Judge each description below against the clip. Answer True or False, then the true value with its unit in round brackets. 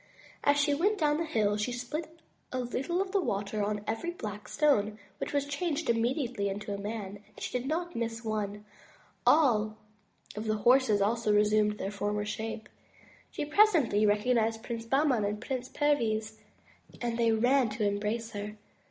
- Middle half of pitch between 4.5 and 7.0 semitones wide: True (4.9 semitones)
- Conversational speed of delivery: True (175 wpm)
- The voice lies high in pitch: True (225 Hz)